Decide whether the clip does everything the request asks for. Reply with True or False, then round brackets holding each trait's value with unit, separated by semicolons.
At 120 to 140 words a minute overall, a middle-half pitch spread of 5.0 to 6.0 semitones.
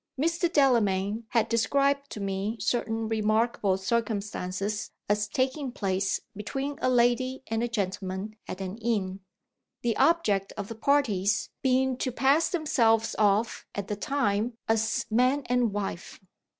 False (135 wpm; 4.1 semitones)